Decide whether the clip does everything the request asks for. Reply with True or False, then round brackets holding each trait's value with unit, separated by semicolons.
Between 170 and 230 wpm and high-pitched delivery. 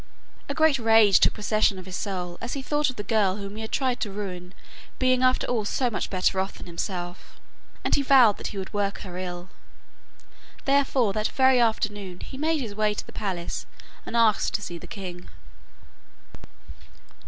True (190 wpm; 210 Hz)